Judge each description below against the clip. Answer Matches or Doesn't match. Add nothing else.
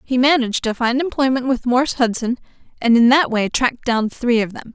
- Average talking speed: Doesn't match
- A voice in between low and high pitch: Doesn't match